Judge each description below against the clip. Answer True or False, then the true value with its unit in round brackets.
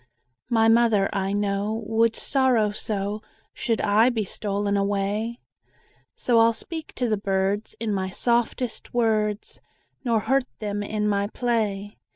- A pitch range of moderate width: False (2.3 semitones)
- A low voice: False (215 Hz)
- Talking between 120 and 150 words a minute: True (140 wpm)